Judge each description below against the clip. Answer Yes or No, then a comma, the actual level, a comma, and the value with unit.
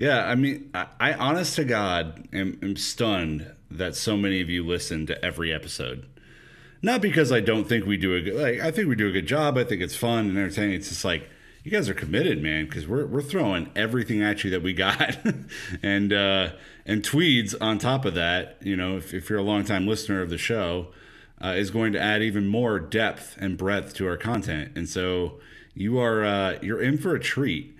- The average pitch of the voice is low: Yes, low, 100 Hz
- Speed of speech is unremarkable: No, fast, 220 wpm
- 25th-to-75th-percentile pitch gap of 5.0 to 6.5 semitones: No, average, 3.6 semitones